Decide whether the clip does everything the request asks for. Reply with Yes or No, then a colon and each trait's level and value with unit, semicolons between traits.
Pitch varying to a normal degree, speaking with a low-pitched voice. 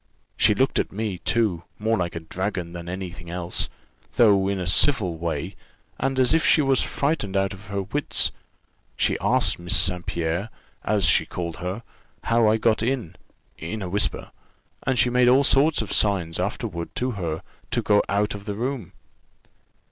Yes: average, 4.7 semitones; low, 100 Hz